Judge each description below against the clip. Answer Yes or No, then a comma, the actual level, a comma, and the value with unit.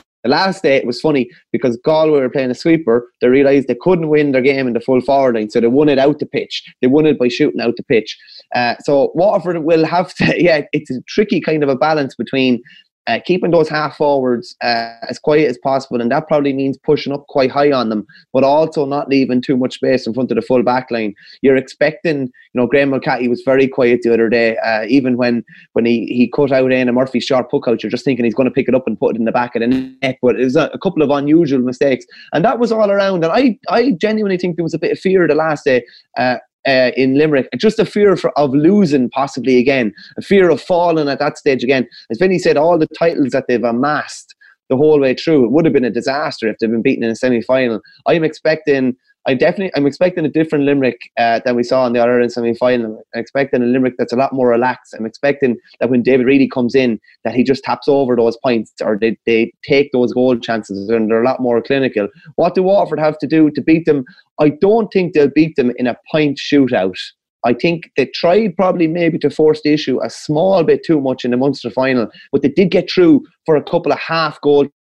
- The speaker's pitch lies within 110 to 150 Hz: Yes, low, 135 Hz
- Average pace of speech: No, fast, 245 wpm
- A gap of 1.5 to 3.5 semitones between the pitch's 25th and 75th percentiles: No, average, 4.1 semitones